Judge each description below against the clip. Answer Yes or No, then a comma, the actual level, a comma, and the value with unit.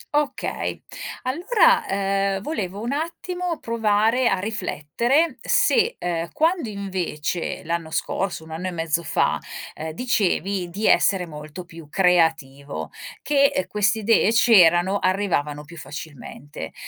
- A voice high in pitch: Yes, high, 195 Hz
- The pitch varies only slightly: No, wide, 6.0 semitones